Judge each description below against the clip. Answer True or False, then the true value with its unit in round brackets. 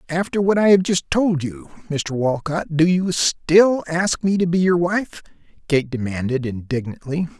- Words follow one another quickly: False (170 wpm)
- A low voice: False (165 Hz)